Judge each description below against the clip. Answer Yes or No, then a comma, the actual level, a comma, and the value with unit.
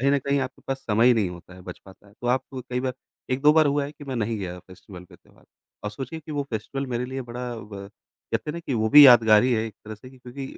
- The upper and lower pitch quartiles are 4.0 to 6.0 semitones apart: Yes, average, 4.4 semitones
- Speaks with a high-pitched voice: No, low, 125 Hz